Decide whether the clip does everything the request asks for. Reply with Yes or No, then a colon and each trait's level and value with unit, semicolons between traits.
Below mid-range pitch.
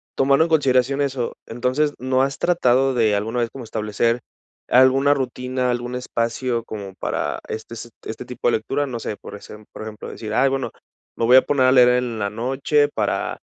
Yes: low, 125 Hz